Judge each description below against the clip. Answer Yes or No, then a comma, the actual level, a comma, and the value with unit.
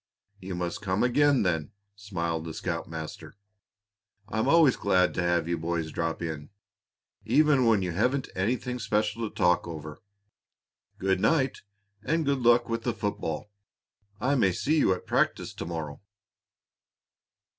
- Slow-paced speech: No, average, 145 wpm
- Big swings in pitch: Yes, wide, 6.5 semitones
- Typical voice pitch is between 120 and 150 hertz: No, very low, 95 Hz